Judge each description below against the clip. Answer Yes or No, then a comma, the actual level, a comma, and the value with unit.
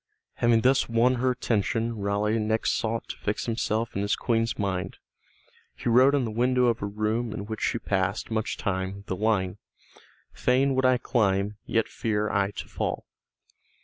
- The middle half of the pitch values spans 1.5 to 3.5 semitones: Yes, narrow, 2.6 semitones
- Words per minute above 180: No, average, 175 wpm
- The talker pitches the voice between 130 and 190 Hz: No, low, 110 Hz